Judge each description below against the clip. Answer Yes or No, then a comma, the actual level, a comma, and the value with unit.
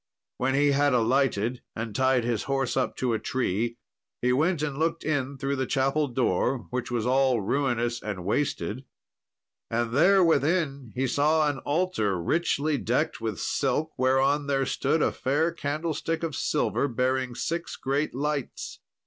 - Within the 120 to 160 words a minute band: Yes, average, 155 wpm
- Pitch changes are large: No, average, 3.3 semitones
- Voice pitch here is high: No, low, 135 Hz